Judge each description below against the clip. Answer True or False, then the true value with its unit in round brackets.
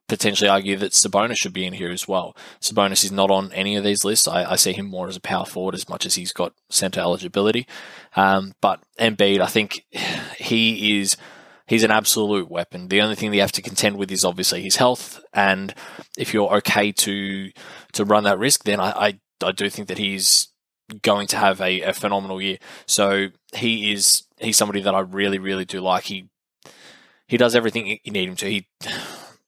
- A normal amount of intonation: False (1.5 semitones)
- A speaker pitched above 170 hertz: False (100 Hz)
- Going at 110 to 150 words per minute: False (200 wpm)